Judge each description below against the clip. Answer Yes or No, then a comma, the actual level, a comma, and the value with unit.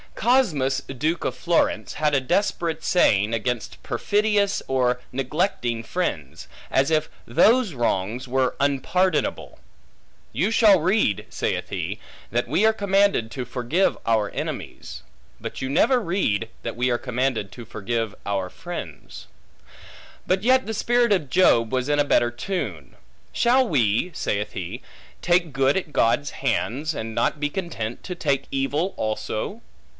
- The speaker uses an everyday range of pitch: No, wide, 7.6 semitones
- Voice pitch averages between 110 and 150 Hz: Yes, medium, 140 Hz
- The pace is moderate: Yes, average, 145 wpm